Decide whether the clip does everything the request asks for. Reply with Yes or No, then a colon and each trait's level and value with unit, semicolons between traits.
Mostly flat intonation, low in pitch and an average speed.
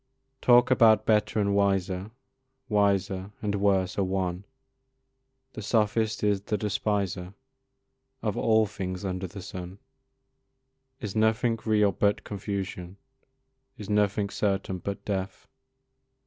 No: narrow, 1.9 semitones; low, 100 Hz; slow, 115 wpm